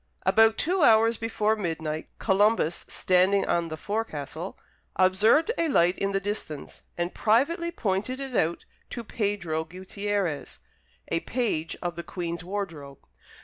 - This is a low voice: No, high, 195 Hz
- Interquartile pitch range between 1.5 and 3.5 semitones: No, average, 4.6 semitones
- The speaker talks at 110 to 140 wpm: Yes, slow, 135 wpm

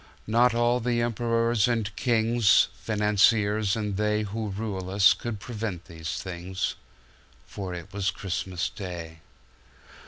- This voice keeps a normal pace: No, slow, 115 wpm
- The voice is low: Yes, low, 105 Hz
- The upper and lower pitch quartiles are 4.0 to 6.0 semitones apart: No, average, 3.4 semitones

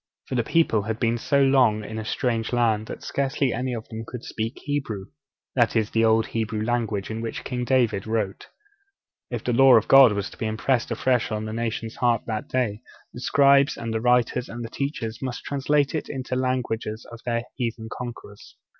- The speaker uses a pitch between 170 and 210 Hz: No, low, 115 Hz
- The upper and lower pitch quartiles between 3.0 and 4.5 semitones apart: No, narrow, 2.6 semitones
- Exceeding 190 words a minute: Yes, average, 200 wpm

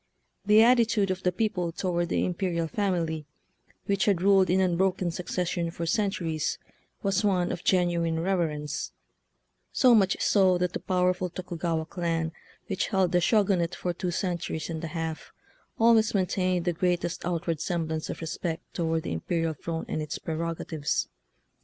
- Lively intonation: No, narrow, 2.4 semitones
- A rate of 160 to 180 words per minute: Yes, average, 165 wpm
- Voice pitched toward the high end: No, medium, 175 Hz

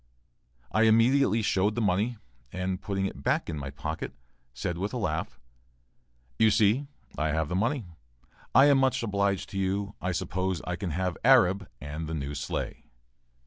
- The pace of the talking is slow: No, average, 170 wpm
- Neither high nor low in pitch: No, very low, 95 Hz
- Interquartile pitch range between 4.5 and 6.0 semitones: Yes, average, 5.3 semitones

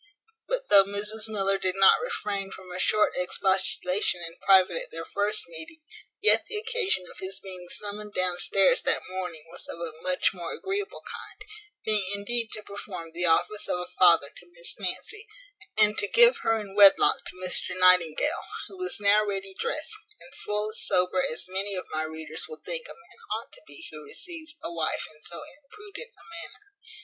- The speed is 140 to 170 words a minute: No, average, 190 wpm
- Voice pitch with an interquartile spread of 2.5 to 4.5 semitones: No, average, 5.2 semitones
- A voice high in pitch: Yes, high, 195 Hz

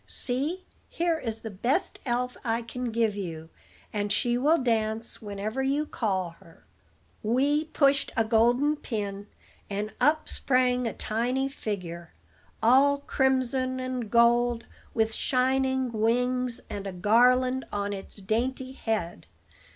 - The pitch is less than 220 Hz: No, high, 240 Hz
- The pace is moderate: No, slow, 130 wpm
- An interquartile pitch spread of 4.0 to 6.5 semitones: No, average, 3.4 semitones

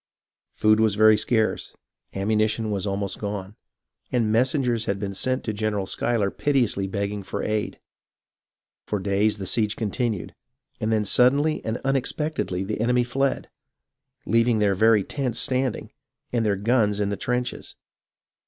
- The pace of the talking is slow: No, average, 145 wpm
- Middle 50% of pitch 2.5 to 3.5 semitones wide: Yes, average, 3.2 semitones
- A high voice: No, low, 110 Hz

